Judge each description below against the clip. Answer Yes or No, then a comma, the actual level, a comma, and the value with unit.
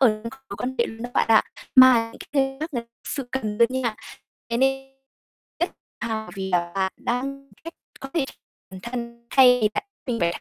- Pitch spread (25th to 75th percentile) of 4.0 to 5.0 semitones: No, average, 3.3 semitones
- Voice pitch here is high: Yes, high, 240 Hz